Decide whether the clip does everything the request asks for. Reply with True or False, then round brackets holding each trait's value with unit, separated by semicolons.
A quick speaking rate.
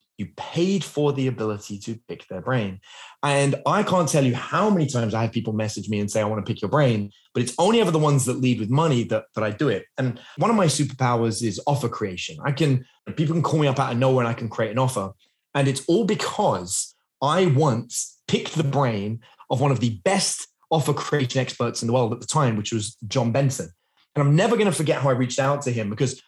True (250 wpm)